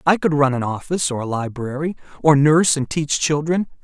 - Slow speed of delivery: No, fast, 205 wpm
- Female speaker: No, male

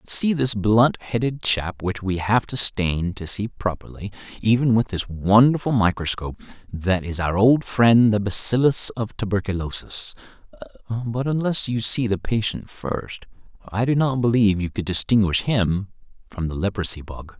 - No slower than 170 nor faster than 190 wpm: No, average, 160 wpm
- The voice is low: Yes, low, 105 Hz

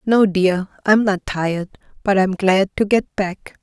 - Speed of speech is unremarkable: Yes, average, 165 wpm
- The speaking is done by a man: No, female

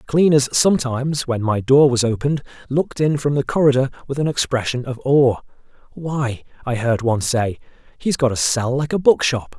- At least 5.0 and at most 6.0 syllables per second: Yes, 5.4 syllables/s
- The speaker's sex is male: Yes, male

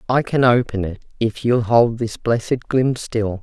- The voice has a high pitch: No, low, 115 Hz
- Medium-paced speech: Yes, average, 190 wpm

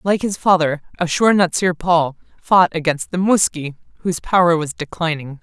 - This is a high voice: No, medium, 170 Hz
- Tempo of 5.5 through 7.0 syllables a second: No, 5.0 syllables/s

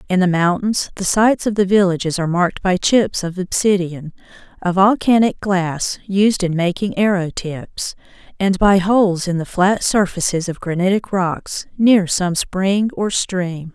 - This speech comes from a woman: Yes, female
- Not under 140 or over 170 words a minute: Yes, average, 160 wpm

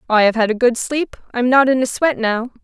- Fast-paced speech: Yes, fast, 275 wpm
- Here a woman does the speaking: Yes, female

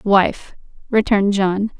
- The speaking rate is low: Yes, slow, 100 wpm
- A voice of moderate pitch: No, high, 200 Hz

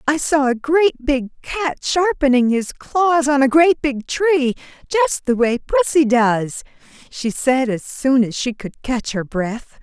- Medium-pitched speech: No, very high, 260 Hz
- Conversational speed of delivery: Yes, average, 175 wpm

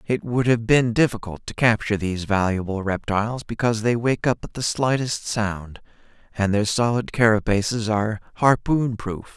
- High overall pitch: No, low, 110 Hz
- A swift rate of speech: No, average, 160 wpm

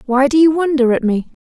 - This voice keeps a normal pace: No, fast, 250 wpm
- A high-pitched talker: Yes, very high, 275 Hz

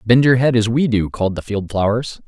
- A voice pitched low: Yes, low, 115 Hz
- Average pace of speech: No, fast, 265 wpm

